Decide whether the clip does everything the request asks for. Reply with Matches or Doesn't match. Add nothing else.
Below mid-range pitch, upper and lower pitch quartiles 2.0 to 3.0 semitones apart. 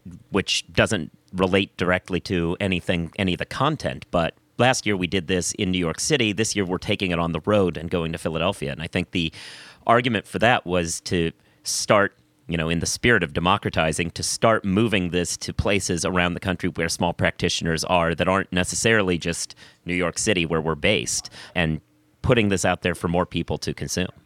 Matches